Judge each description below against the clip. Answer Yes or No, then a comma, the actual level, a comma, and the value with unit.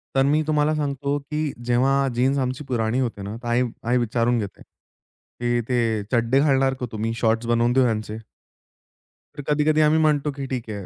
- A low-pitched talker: Yes, low, 125 Hz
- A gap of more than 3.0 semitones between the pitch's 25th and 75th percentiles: Yes, average, 3.4 semitones